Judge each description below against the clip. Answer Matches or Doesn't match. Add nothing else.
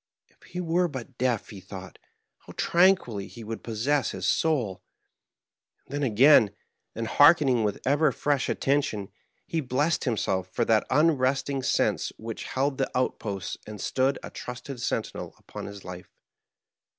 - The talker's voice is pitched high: Doesn't match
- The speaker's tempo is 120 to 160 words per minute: Matches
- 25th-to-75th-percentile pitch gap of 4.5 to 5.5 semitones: Matches